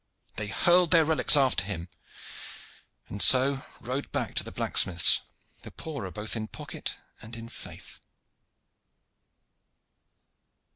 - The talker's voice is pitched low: Yes, low, 115 Hz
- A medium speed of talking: No, slow, 115 wpm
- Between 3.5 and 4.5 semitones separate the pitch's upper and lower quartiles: No, wide, 5.4 semitones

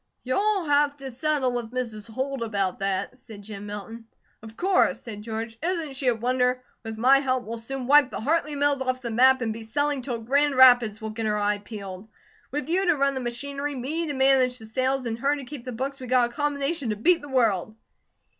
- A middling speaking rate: No, fast, 220 wpm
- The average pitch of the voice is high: Yes, very high, 255 Hz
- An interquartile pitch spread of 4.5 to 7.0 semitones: No, average, 4.0 semitones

